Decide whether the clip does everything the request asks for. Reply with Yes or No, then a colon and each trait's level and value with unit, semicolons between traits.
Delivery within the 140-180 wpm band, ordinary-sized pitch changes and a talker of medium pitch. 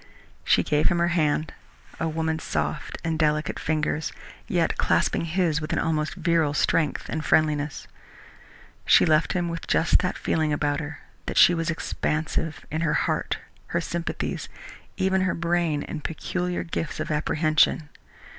No: average, 155 wpm; narrow, 1.7 semitones; medium, 160 Hz